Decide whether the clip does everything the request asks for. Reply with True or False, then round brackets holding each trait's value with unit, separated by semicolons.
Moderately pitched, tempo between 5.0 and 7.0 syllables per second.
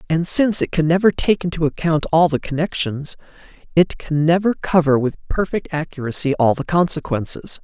True (160 Hz; 5.4 syllables/s)